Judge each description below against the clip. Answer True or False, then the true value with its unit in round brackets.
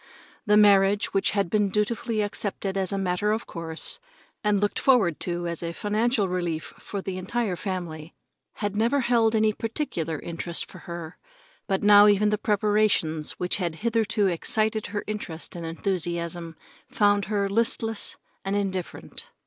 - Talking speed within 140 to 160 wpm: True (155 wpm)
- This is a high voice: True (200 Hz)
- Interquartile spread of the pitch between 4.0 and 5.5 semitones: False (3.5 semitones)